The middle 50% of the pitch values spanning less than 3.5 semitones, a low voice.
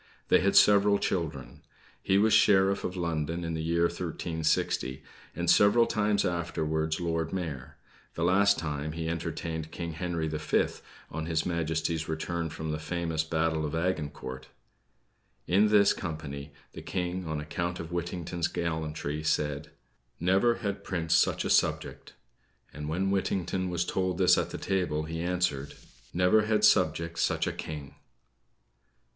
Yes: narrow, 2.6 semitones; very low, 85 Hz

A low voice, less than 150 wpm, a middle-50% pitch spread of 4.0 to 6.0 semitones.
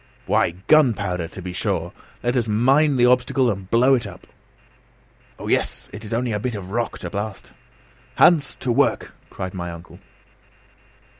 No: low, 115 Hz; average, 165 wpm; average, 4.6 semitones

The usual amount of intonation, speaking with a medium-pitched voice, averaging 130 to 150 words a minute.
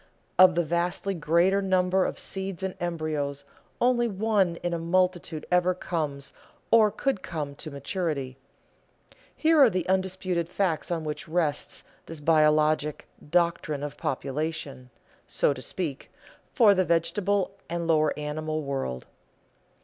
Yes: average, 3.5 semitones; medium, 170 Hz; slow, 135 wpm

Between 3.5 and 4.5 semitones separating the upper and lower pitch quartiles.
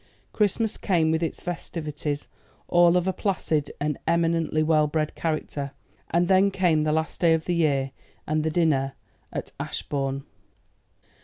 No: narrow, 2.5 semitones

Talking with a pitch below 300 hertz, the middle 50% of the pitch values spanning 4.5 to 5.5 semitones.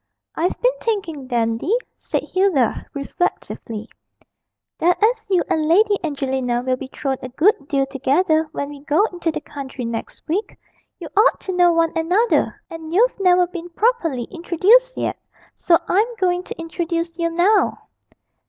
No: very high, 335 Hz; average, 5.2 semitones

